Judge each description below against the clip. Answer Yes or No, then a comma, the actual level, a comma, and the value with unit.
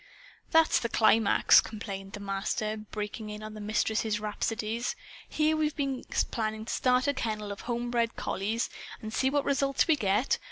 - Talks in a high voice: Yes, high, 220 Hz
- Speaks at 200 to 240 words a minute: No, average, 170 wpm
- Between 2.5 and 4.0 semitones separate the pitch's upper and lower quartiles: Yes, average, 3.3 semitones